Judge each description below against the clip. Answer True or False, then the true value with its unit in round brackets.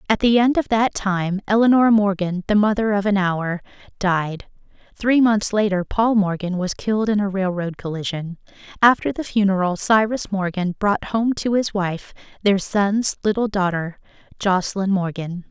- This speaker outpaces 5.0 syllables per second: False (4.7 syllables/s)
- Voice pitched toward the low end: False (200 Hz)